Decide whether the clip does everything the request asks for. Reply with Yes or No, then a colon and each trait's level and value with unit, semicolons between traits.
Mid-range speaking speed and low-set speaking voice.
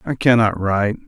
Yes: average, 165 wpm; low, 110 Hz